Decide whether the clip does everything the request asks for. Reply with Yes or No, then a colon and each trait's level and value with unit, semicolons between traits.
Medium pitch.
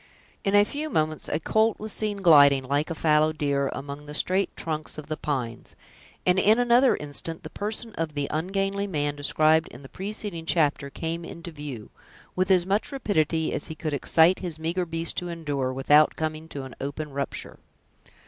Yes: medium, 160 Hz